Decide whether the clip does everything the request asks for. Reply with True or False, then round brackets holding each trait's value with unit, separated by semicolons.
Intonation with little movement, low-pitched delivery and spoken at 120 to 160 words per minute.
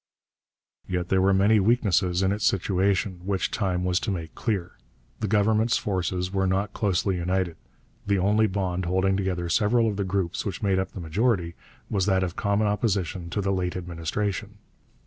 False (2.1 semitones; 95 Hz; 175 wpm)